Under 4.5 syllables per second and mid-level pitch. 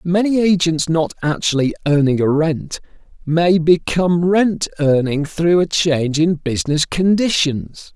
Yes: 4.2 syllables/s; medium, 165 Hz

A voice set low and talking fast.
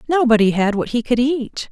No: high, 240 Hz; fast, 210 wpm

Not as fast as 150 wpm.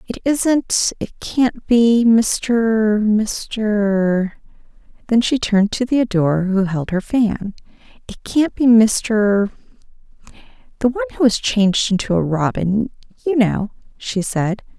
Yes: slow, 135 wpm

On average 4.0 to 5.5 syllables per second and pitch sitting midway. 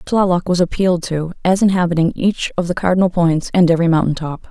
No: 6.1 syllables/s; medium, 175 Hz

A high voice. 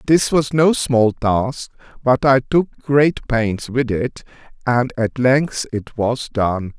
No: low, 125 Hz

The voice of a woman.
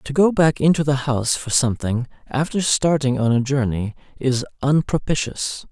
No: male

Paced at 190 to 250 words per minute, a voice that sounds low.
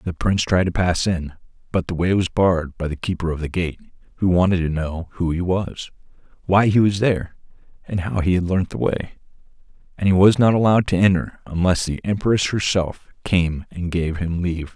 Yes: fast, 205 wpm; very low, 90 Hz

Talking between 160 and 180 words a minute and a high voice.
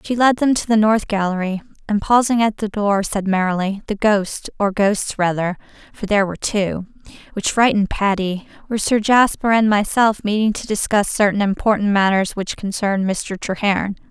Yes: average, 165 wpm; high, 205 Hz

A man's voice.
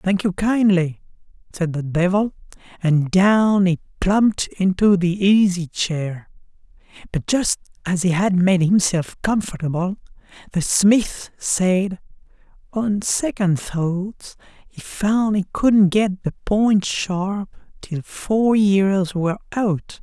Yes: male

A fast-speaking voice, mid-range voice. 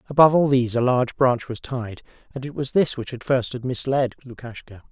No: fast, 220 wpm; low, 125 Hz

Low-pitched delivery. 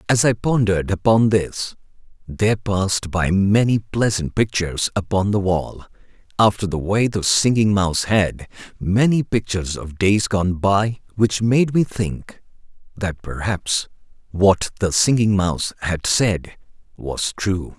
Yes: low, 100 Hz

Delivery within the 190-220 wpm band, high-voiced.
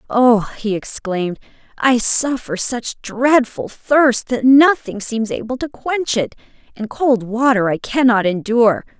No: average, 140 wpm; high, 235 Hz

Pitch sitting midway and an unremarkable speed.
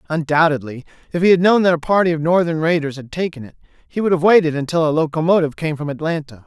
No: medium, 160 Hz; fast, 225 wpm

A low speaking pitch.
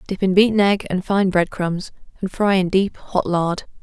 No: high, 190 Hz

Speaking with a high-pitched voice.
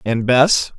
No: low, 130 Hz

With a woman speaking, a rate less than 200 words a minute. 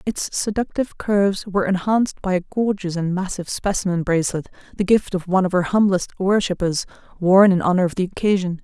Yes: female; average, 180 wpm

